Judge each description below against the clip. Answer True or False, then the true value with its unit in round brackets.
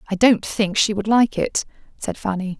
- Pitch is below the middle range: False (200 Hz)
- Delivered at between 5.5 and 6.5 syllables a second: False (4.9 syllables/s)